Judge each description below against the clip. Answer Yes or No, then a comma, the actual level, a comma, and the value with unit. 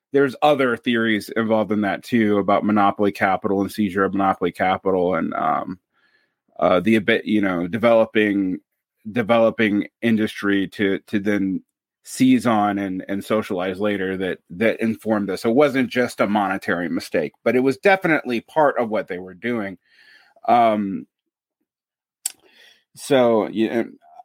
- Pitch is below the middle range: Yes, low, 110 Hz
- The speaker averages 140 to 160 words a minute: Yes, average, 145 wpm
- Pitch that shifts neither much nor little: Yes, average, 3.4 semitones